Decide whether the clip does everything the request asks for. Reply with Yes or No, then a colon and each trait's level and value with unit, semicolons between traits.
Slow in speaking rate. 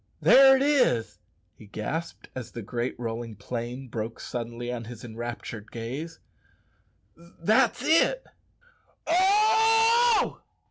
Yes: slow, 105 wpm